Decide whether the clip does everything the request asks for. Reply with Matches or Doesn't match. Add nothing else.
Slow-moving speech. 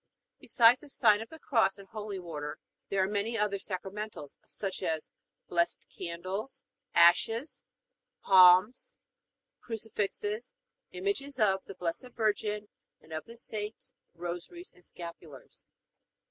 Matches